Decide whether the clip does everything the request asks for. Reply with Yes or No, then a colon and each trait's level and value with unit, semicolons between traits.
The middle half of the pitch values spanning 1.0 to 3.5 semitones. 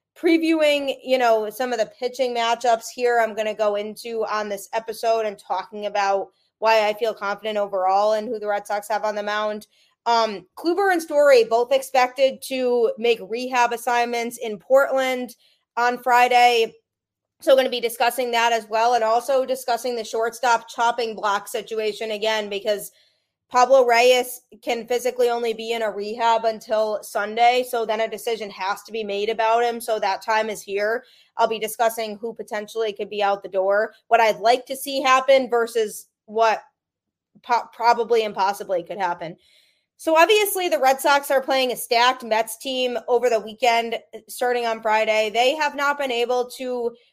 Yes: narrow, 2.5 semitones